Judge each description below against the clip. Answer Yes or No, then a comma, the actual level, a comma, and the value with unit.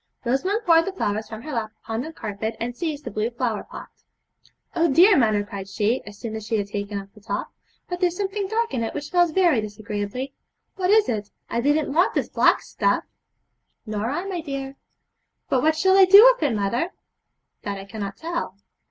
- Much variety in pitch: Yes, wide, 8.3 semitones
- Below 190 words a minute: No, fast, 205 wpm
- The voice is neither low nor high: No, very high, 250 Hz